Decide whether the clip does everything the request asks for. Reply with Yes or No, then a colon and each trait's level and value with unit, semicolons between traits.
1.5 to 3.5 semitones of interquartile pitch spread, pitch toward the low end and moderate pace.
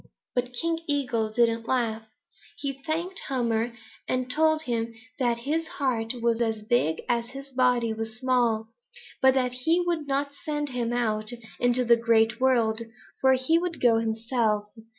No: average, 3.1 semitones; high, 245 Hz; average, 155 wpm